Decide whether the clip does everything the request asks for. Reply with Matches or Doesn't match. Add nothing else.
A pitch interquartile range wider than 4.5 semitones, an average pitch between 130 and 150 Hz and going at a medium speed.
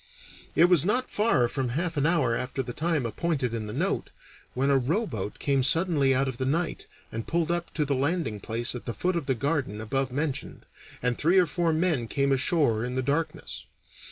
Doesn't match